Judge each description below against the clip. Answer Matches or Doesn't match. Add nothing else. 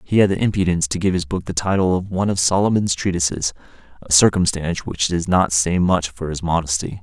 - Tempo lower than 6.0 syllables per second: Doesn't match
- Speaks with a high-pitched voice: Doesn't match